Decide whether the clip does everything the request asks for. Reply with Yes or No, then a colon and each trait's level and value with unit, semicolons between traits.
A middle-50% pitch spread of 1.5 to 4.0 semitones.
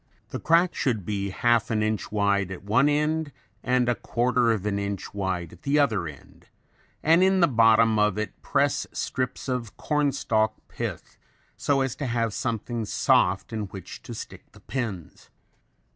No: average, 4.7 semitones